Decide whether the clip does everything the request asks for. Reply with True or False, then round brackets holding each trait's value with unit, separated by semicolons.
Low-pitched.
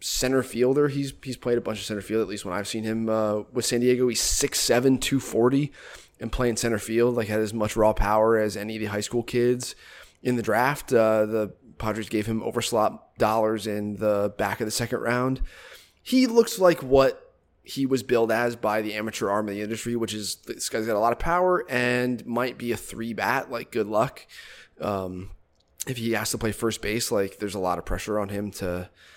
True (115 Hz)